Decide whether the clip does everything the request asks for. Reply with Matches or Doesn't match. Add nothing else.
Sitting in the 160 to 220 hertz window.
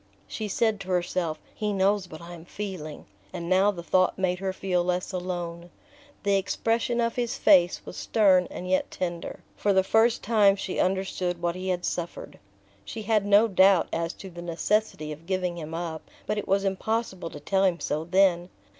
Matches